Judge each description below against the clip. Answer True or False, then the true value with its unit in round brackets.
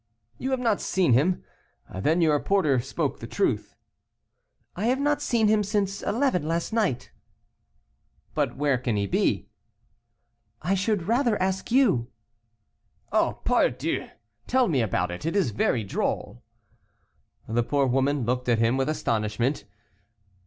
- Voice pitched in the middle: True (155 Hz)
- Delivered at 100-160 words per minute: True (140 wpm)